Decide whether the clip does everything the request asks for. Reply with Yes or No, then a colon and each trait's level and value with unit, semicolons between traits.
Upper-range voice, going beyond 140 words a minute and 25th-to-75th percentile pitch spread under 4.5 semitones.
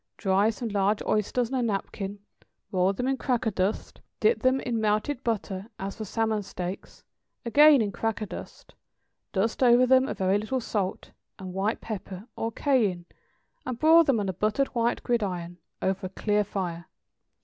Yes: high, 215 Hz; average, 170 wpm; average, 3.9 semitones